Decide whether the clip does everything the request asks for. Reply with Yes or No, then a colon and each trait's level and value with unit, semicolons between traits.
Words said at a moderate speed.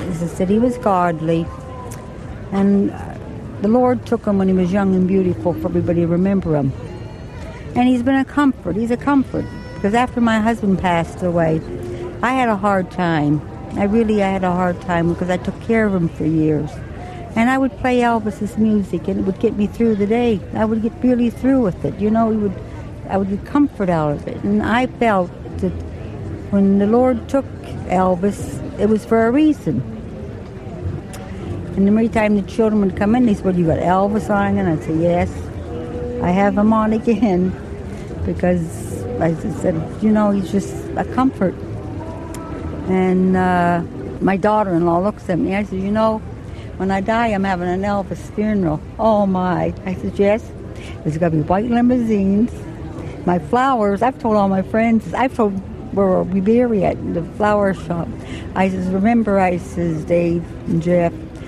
Yes: average, 185 wpm